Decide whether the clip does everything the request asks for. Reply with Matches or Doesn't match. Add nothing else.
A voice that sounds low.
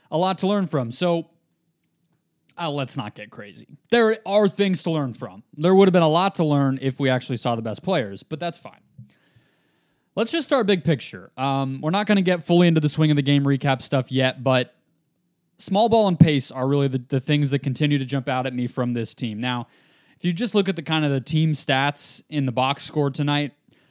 Doesn't match